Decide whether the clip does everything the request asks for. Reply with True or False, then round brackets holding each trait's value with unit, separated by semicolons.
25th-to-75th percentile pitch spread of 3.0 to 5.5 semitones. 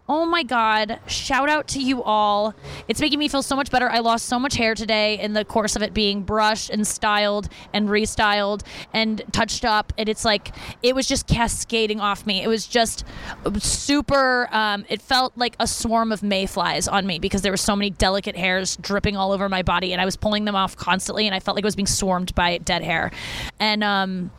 False (2.6 semitones)